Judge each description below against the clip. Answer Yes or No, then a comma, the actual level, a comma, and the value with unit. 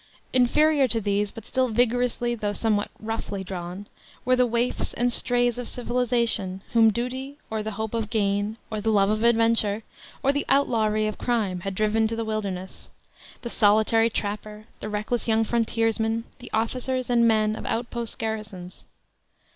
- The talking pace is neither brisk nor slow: Yes, average, 165 wpm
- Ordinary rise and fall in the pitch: No, narrow, 2.3 semitones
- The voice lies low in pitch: No, high, 225 Hz